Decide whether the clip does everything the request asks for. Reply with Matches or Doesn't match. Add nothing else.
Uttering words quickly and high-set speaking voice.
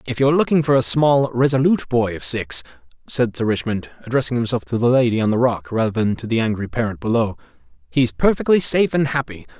Doesn't match